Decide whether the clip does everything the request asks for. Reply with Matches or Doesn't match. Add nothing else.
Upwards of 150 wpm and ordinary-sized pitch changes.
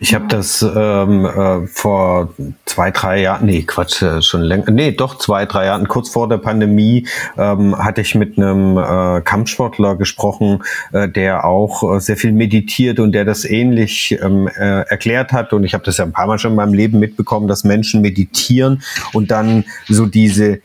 Doesn't match